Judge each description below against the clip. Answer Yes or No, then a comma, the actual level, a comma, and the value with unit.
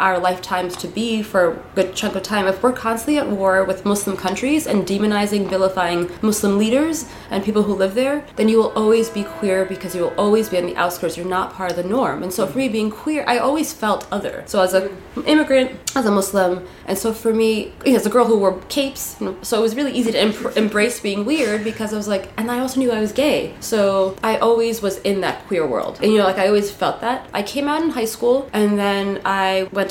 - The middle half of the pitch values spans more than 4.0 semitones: No, average, 3.5 semitones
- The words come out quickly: Yes, fast, 245 wpm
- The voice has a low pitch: No, high, 210 Hz